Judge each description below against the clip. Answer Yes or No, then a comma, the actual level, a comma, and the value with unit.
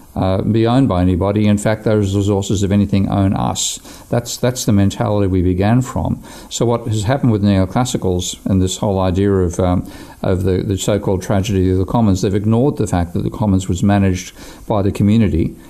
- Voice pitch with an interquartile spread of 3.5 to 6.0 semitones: No, narrow, 2.6 semitones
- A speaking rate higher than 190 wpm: Yes, fast, 205 wpm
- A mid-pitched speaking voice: No, low, 100 Hz